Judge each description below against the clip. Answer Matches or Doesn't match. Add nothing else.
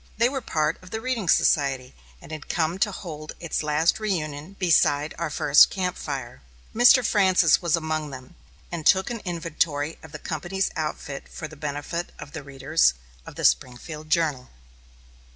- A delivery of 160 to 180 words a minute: Matches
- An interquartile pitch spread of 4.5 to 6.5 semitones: Doesn't match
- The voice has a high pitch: Doesn't match